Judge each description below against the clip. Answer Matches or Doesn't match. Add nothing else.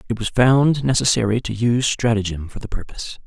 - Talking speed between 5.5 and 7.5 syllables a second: Matches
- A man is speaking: Matches